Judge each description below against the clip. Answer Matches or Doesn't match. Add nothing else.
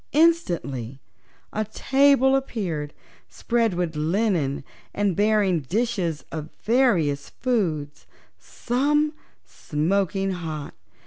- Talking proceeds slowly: Matches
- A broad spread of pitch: Matches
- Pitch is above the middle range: Matches